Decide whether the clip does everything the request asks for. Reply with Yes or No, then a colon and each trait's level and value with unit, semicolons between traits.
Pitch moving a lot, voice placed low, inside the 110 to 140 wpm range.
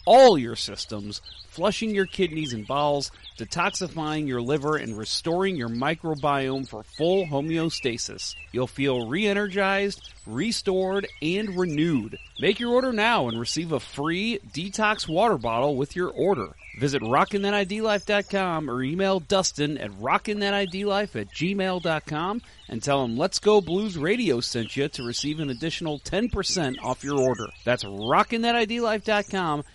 No: wide, 7.5 semitones; medium, 160 Hz; slow, 135 wpm